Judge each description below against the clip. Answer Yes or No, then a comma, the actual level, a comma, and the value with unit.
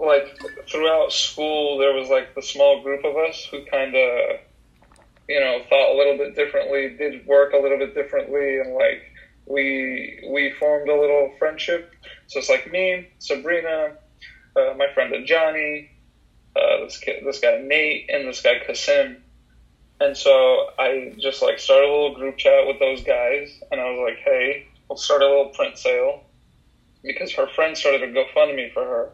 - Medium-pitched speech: Yes, medium, 160 Hz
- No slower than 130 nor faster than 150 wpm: No, average, 185 wpm